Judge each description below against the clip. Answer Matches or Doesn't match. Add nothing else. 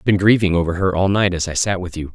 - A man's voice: Matches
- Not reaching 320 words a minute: Doesn't match